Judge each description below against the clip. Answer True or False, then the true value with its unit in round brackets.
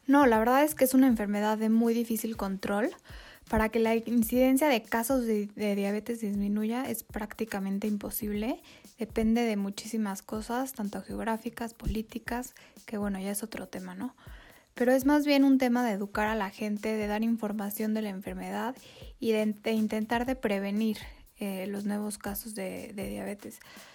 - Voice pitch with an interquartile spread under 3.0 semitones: True (2.4 semitones)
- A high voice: True (220 Hz)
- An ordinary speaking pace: True (175 wpm)